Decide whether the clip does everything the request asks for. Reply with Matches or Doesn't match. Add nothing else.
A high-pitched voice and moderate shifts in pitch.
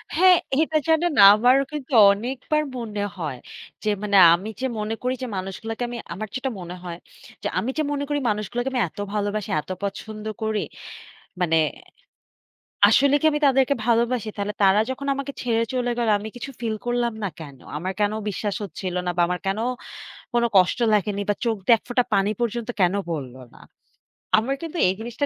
Matches